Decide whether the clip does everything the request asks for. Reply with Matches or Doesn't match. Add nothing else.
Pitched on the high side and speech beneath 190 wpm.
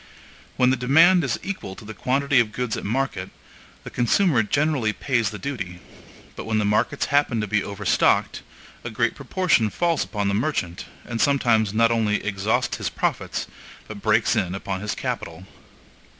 Doesn't match